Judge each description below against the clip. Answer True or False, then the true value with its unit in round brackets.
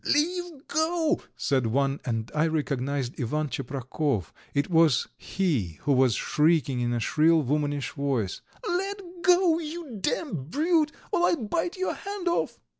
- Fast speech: False (145 wpm)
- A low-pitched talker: False (155 Hz)